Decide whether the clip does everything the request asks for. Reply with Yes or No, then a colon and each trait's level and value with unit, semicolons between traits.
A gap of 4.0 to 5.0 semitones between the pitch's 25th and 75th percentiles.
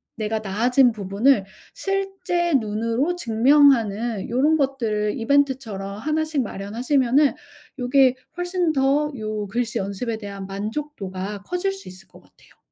No: wide, 5.4 semitones